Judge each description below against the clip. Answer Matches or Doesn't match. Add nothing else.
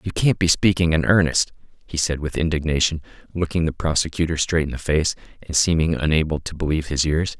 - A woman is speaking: Doesn't match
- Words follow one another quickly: Doesn't match